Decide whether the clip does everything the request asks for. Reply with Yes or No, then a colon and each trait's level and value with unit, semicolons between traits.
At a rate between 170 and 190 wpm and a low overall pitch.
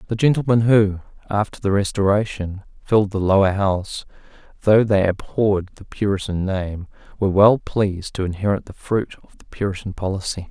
No: average, 155 wpm; low, 100 Hz